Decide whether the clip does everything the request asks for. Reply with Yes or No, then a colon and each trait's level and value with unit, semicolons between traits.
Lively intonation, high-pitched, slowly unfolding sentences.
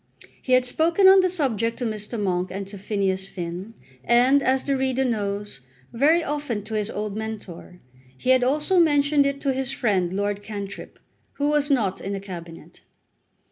No: wide, 5.7 semitones; high, 230 Hz; average, 180 wpm